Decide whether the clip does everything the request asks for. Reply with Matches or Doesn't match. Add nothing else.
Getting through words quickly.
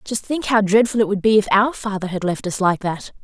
Matches